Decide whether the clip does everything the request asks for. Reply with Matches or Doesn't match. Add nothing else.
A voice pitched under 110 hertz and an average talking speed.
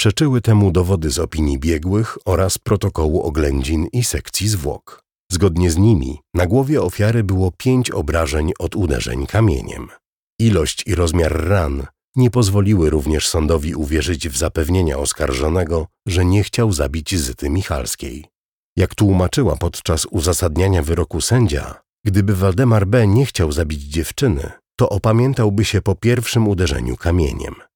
Matches